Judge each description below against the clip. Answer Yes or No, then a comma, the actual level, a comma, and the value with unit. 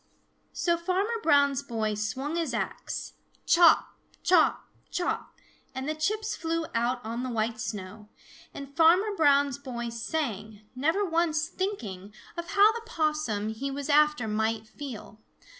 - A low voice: No, very high, 280 Hz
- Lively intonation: Yes, wide, 6.7 semitones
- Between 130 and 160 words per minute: Yes, average, 140 wpm